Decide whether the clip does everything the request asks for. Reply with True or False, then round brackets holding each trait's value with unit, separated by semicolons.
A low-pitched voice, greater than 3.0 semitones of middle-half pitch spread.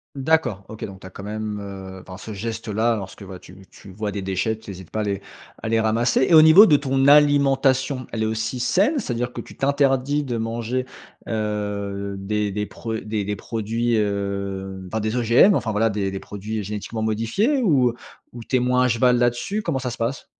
True (110 Hz; 3.9 semitones)